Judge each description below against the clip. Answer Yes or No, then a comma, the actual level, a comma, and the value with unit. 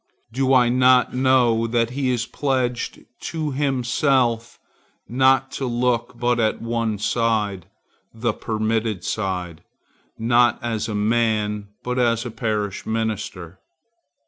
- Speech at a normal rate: No, slow, 120 wpm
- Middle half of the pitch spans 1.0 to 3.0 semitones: Yes, narrow, 2.5 semitones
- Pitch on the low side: Yes, low, 115 Hz